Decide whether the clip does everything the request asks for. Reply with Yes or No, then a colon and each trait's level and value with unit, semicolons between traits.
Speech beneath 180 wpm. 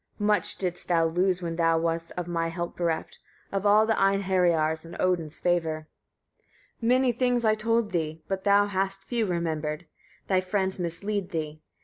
Yes: average, 165 wpm